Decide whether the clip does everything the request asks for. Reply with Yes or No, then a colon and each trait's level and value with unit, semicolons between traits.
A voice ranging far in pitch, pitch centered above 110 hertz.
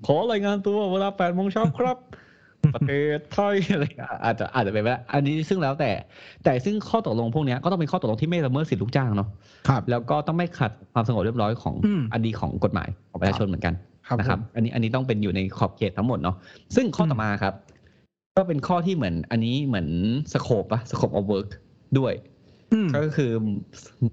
Yes: wide, 7.1 semitones; low, 125 Hz